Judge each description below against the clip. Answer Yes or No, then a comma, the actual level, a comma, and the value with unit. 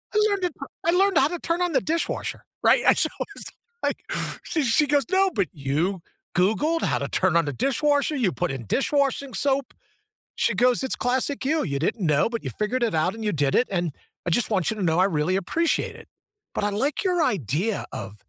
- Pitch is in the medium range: No, high, 235 Hz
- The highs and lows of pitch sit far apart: Yes, wide, 8.7 semitones